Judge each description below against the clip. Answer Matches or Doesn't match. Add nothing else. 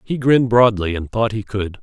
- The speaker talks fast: Matches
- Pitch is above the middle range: Doesn't match